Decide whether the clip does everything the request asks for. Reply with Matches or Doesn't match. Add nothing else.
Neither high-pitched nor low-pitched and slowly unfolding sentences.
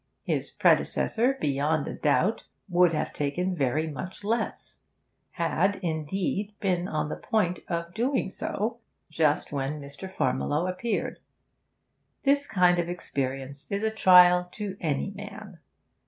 Matches